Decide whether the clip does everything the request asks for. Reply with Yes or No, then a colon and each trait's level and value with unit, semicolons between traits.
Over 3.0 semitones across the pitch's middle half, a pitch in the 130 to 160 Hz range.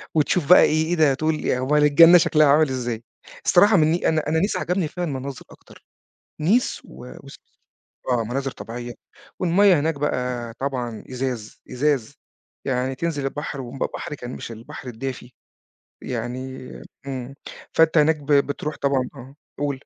Yes: average, 3.8 semitones; medium, 140 Hz